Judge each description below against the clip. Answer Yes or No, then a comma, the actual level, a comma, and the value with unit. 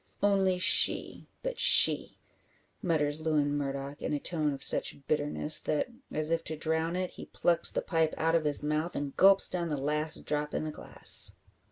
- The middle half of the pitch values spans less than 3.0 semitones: Yes, narrow, 2.4 semitones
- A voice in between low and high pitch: Yes, medium, 155 Hz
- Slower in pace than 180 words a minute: No, average, 185 wpm